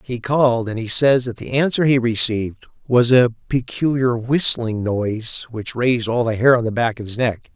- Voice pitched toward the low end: Yes, low, 120 Hz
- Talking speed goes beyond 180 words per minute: Yes, fast, 205 wpm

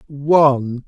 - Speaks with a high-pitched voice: No, medium, 140 Hz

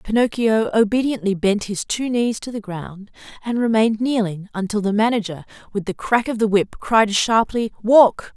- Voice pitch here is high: Yes, high, 215 Hz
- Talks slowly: No, average, 170 wpm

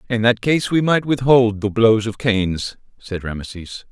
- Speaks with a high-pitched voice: No, low, 115 Hz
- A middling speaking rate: Yes, average, 185 wpm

